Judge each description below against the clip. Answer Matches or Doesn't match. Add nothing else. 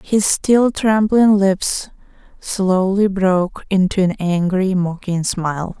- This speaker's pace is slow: Matches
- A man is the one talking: Doesn't match